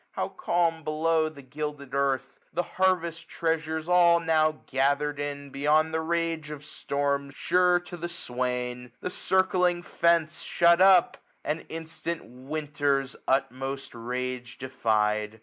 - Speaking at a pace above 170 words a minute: No, slow, 135 wpm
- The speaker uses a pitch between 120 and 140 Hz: No, medium, 155 Hz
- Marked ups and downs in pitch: No, average, 3.9 semitones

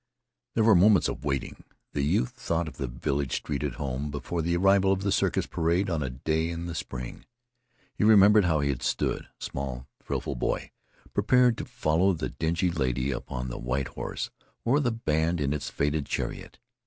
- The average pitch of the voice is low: Yes, very low, 80 Hz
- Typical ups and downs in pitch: No, wide, 5.7 semitones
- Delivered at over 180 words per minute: Yes, average, 190 wpm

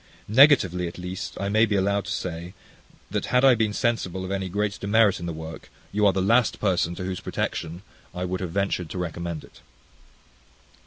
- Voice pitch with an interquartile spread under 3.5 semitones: Yes, average, 2.7 semitones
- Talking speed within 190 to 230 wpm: Yes, average, 200 wpm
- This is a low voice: Yes, very low, 95 Hz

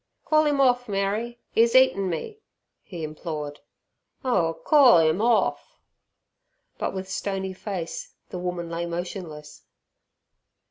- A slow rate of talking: Yes, slow, 120 wpm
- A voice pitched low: No, high, 190 Hz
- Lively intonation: Yes, wide, 5.9 semitones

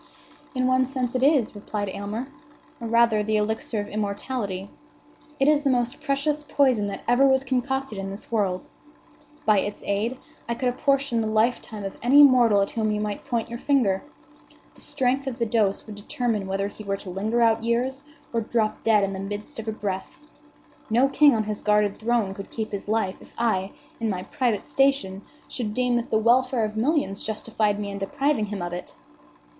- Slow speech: No, average, 195 wpm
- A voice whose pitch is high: Yes, high, 225 Hz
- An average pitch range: Yes, average, 3.7 semitones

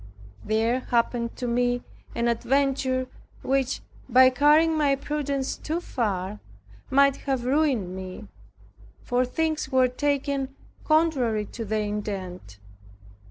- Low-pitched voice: No, very high, 255 Hz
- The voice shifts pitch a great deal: No, average, 3.6 semitones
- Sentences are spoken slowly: Yes, slow, 115 wpm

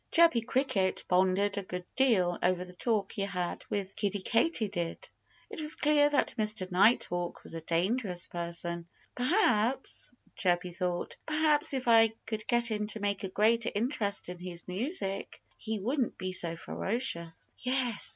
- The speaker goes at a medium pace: Yes, average, 155 wpm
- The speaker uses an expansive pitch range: No, average, 4.9 semitones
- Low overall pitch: No, high, 205 Hz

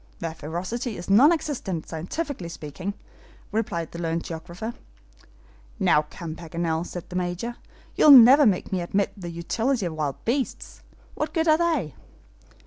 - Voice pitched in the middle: Yes, medium, 180 Hz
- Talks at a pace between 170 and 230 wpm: No, average, 145 wpm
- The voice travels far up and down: Yes, wide, 6.2 semitones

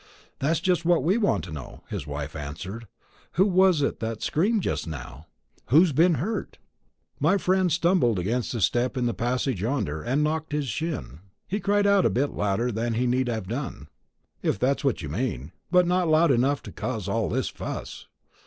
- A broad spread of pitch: Yes, wide, 7.6 semitones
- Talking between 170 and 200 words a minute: Yes, average, 190 wpm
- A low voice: Yes, low, 130 Hz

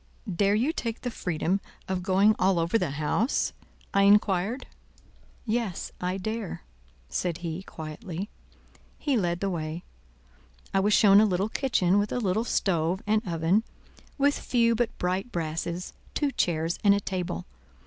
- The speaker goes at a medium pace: Yes, average, 150 wpm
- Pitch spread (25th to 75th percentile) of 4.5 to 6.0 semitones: No, average, 3.9 semitones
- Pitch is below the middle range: No, high, 195 Hz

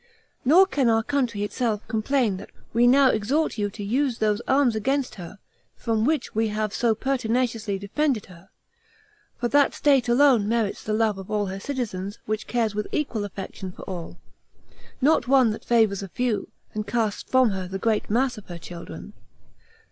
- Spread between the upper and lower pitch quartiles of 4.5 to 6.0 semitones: No, average, 4.0 semitones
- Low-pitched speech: No, high, 225 Hz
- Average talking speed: Yes, average, 180 wpm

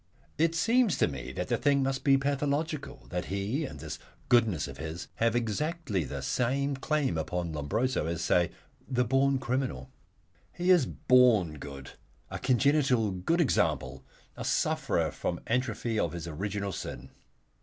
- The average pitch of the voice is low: Yes, low, 120 Hz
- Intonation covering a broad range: Yes, wide, 8.0 semitones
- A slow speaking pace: No, average, 160 wpm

